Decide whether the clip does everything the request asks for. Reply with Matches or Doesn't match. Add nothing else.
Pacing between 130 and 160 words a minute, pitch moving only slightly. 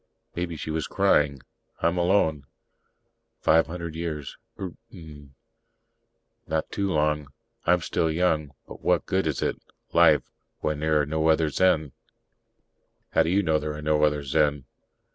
Matches